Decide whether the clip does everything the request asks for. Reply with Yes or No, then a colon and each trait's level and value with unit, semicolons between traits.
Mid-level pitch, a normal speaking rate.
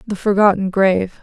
No: high, 195 Hz; average, 145 wpm